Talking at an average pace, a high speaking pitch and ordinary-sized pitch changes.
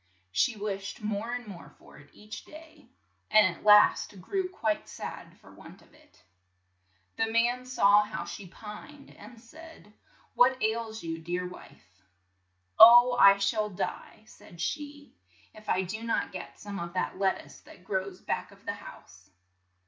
Yes: average, 165 wpm; high, 210 Hz; average, 3.7 semitones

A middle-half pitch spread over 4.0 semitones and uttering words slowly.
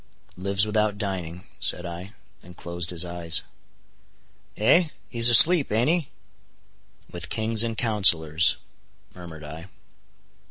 Yes: average, 4.4 semitones; slow, 110 wpm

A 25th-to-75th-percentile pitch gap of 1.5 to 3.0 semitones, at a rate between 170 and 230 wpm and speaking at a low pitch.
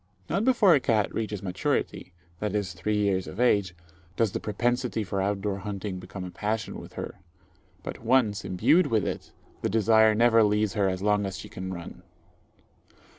Yes: average, 2.7 semitones; average, 175 wpm; low, 105 Hz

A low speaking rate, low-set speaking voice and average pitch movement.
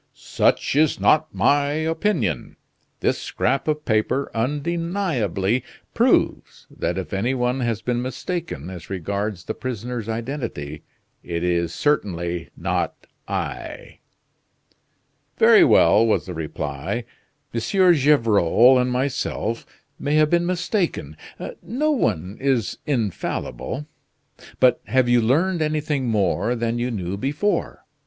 No: slow, 120 wpm; low, 125 Hz; wide, 6.7 semitones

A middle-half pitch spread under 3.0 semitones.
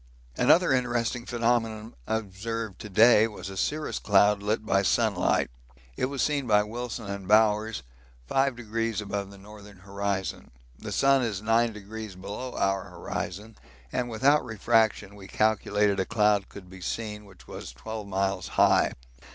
Yes: narrow, 2.4 semitones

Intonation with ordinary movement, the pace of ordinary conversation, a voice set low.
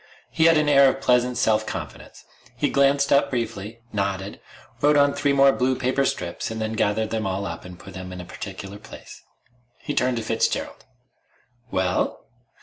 No: wide, 5.8 semitones; average, 180 wpm; low, 110 Hz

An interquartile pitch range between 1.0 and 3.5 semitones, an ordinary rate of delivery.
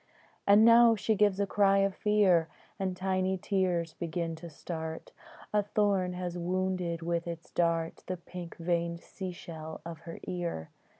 Yes: narrow, 2.5 semitones; average, 160 wpm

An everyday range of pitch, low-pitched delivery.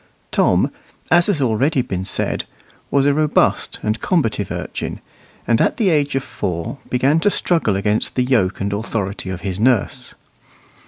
No: wide, 5.9 semitones; low, 120 Hz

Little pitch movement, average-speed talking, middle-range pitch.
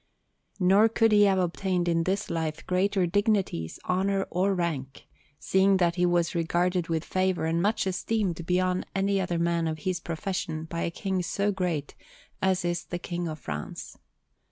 Yes: narrow, 2.3 semitones; average, 170 wpm; medium, 180 Hz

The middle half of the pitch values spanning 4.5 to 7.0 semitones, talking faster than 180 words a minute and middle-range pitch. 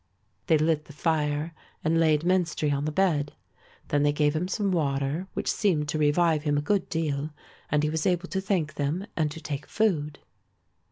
No: average, 2.7 semitones; average, 190 wpm; medium, 155 Hz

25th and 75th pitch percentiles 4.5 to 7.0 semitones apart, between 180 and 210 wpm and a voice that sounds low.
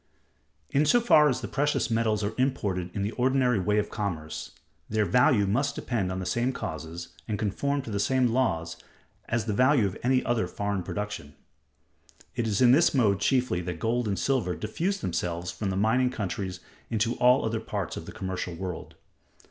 Yes: average, 5.2 semitones; average, 190 wpm; low, 110 Hz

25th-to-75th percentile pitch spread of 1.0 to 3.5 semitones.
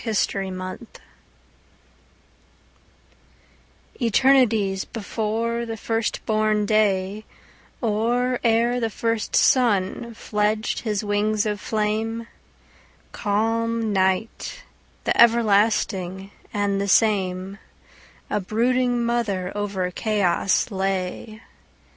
Yes: narrow, 2.5 semitones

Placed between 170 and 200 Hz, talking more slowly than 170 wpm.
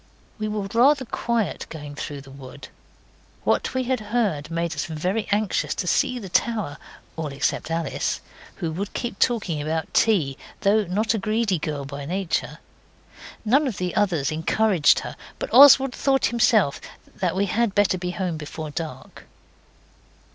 Yes: high, 190 Hz; average, 160 wpm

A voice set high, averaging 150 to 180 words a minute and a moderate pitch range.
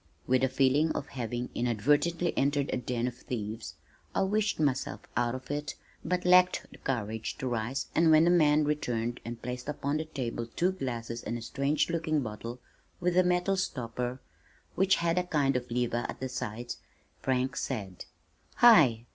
No: low, 130 Hz; average, 175 wpm; average, 4.8 semitones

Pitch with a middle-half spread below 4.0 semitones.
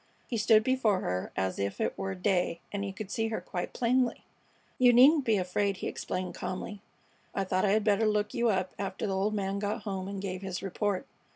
Yes: narrow, 2.6 semitones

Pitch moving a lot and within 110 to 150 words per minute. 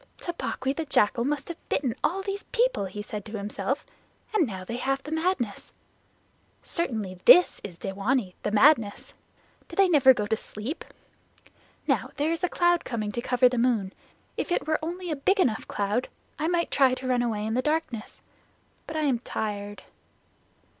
No: wide, 7.1 semitones; average, 175 wpm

